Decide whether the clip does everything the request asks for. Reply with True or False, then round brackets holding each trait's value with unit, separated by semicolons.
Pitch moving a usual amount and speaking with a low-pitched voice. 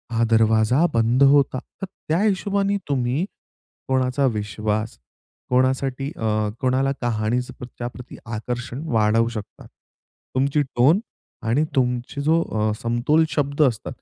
True (3.7 semitones; 125 Hz)